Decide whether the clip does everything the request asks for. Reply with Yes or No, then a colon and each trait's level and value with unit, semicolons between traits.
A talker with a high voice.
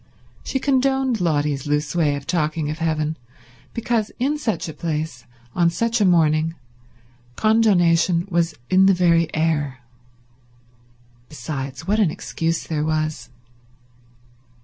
No: medium, 165 Hz